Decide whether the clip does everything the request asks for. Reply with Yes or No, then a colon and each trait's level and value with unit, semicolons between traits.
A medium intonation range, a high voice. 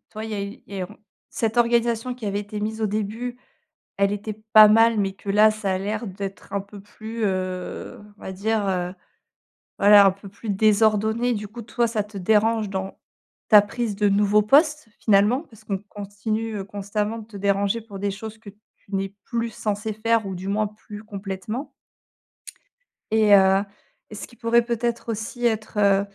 No: narrow, 2.0 semitones; high, 210 Hz